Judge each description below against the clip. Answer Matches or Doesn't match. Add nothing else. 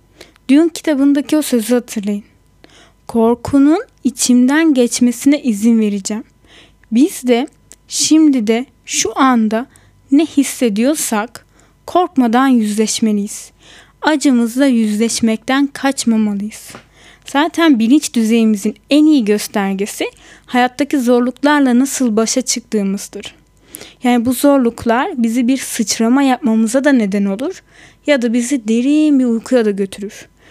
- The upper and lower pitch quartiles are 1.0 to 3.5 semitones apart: Doesn't match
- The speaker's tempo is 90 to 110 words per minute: Matches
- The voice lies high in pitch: Matches